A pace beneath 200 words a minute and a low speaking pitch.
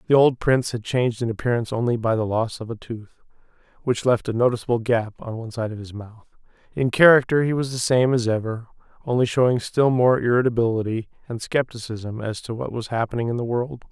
No: fast, 205 wpm; low, 120 Hz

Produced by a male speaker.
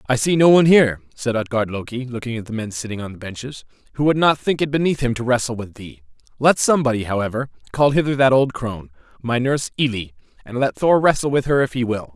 Yes: male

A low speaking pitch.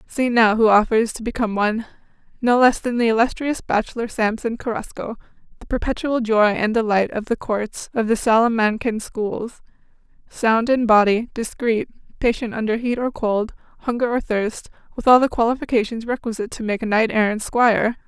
No: high, 225 Hz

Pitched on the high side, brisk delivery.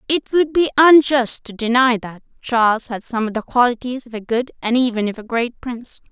Yes: high, 240 Hz; fast, 215 wpm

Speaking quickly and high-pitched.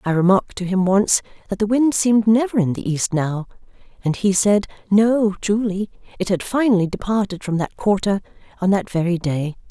No: average, 185 wpm; high, 200 Hz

